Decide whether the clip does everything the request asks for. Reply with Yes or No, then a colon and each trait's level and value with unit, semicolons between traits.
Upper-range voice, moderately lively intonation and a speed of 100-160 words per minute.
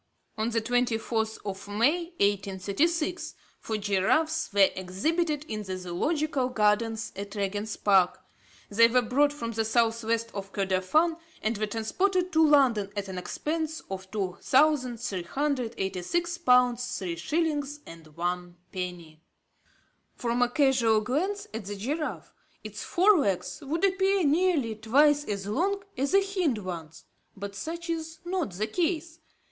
No: high, 230 Hz; wide, 7.5 semitones; average, 140 wpm